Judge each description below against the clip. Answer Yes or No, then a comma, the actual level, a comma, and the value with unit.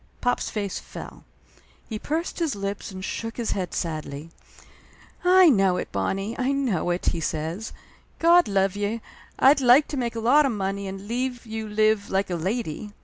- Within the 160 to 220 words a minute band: Yes, average, 180 wpm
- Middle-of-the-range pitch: No, high, 215 Hz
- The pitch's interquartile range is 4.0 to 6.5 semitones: Yes, average, 4.5 semitones